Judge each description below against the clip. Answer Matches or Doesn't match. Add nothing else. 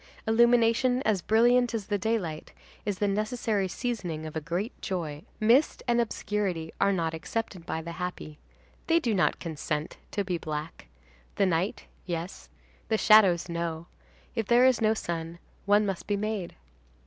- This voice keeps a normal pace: Matches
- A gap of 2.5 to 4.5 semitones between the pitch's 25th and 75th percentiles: Doesn't match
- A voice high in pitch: Matches